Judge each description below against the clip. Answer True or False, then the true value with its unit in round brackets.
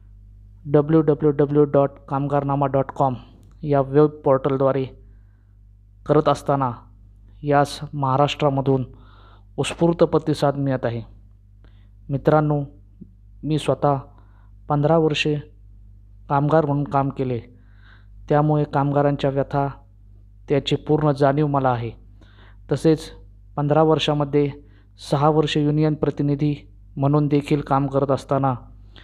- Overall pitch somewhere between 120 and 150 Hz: True (140 Hz)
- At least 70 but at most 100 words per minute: True (95 wpm)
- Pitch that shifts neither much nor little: False (6.5 semitones)